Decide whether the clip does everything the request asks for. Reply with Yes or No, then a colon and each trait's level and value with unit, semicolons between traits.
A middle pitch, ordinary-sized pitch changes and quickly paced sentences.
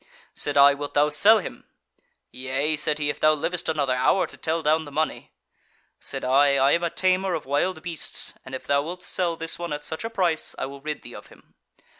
Yes: medium, 155 Hz; average, 3.2 semitones; fast, 225 wpm